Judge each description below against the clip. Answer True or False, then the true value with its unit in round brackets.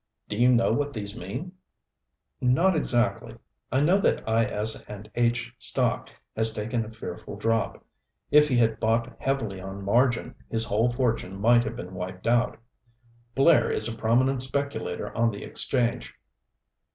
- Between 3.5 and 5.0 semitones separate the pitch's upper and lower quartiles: False (2.7 semitones)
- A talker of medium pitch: False (115 Hz)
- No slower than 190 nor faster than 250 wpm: False (160 wpm)